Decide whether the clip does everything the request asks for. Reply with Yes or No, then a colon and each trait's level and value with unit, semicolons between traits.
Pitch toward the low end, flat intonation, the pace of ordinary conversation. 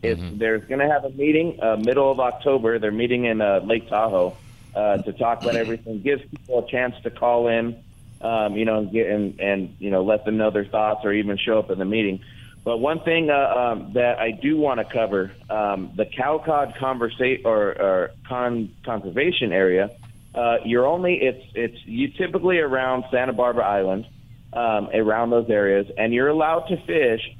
No: low, 115 Hz; average, 3.2 semitones; average, 195 wpm